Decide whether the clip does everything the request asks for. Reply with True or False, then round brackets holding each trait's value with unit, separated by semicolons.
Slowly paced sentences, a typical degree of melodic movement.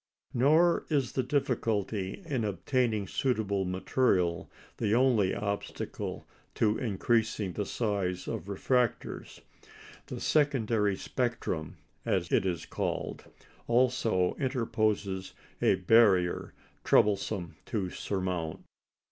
True (95 wpm; 4.7 semitones)